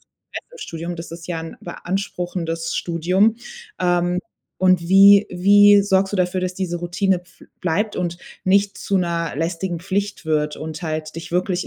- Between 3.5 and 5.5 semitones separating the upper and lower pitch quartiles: No, narrow, 2.4 semitones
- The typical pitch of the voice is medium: Yes, medium, 180 Hz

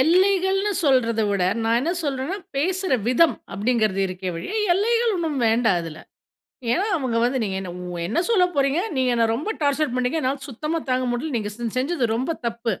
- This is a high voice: Yes, very high, 265 Hz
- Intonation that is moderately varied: No, wide, 6.5 semitones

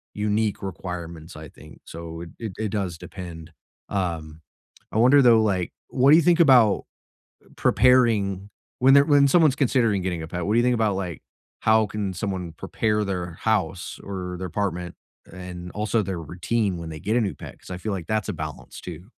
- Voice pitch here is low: Yes, low, 100 Hz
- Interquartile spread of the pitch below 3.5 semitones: No, average, 4.1 semitones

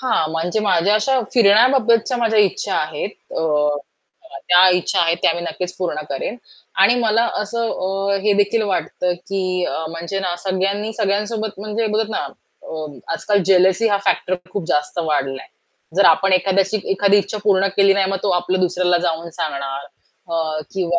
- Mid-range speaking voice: No, high, 195 Hz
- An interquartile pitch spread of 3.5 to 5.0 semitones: No, average, 3.1 semitones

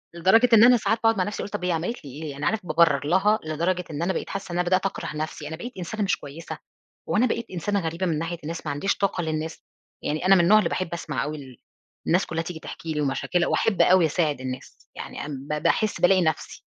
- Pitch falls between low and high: Yes, medium, 170 Hz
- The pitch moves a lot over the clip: No, average, 3.9 semitones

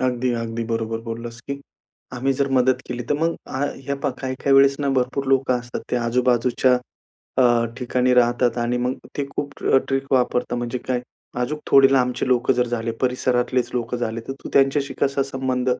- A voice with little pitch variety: Yes, narrow, 1.8 semitones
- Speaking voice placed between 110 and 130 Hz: Yes, low, 125 Hz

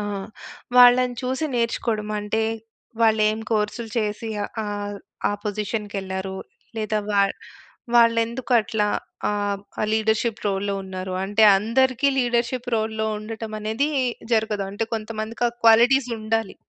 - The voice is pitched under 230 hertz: Yes, high, 220 Hz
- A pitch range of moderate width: No, narrow, 2.0 semitones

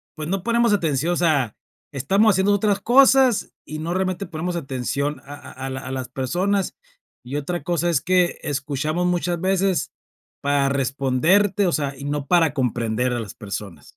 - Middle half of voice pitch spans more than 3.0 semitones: Yes, wide, 5.5 semitones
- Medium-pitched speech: Yes, medium, 155 Hz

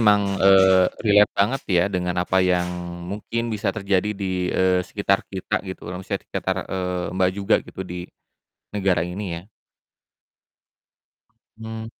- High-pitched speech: No, very low, 95 Hz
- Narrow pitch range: Yes, narrow, 2.2 semitones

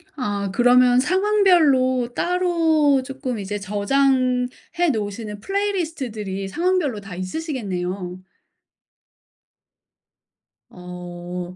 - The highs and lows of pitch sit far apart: Yes, wide, 7.9 semitones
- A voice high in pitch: Yes, very high, 250 Hz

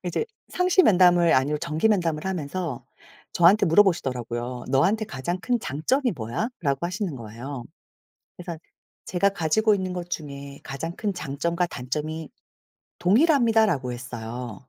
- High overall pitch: No, medium, 170 Hz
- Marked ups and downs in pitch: Yes, wide, 6.1 semitones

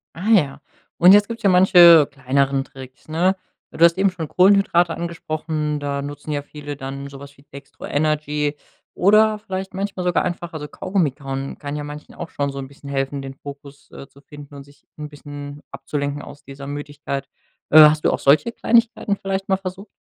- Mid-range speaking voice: Yes, medium, 150 Hz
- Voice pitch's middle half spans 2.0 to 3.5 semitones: No, average, 4.3 semitones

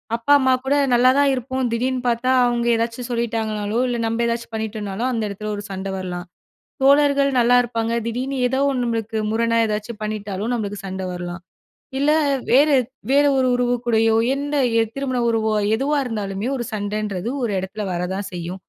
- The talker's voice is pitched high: Yes, high, 230 Hz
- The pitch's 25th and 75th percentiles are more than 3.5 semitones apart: No, average, 3.1 semitones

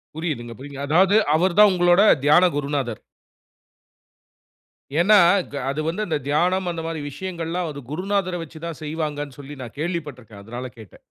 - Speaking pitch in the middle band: Yes, medium, 160 Hz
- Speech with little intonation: No, average, 3.8 semitones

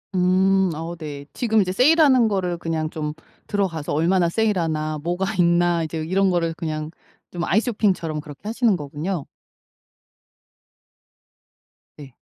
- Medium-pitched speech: Yes, medium, 175 Hz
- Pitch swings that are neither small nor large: Yes, average, 3.6 semitones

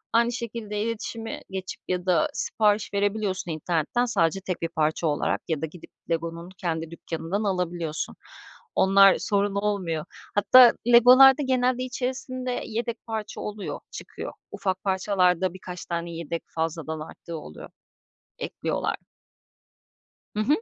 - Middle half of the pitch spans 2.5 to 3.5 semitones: No, average, 5.0 semitones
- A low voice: No, high, 190 Hz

